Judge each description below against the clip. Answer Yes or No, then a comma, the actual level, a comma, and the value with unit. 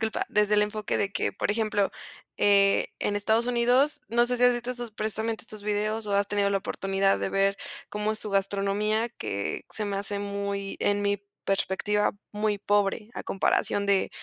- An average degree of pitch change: No, narrow, 1.6 semitones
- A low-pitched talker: No, high, 205 Hz